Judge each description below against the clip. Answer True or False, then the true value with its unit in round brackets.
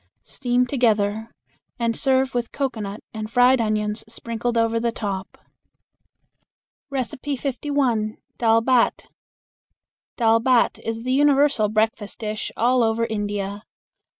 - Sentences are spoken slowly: True (110 wpm)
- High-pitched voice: True (230 Hz)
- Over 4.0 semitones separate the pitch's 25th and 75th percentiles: False (2.8 semitones)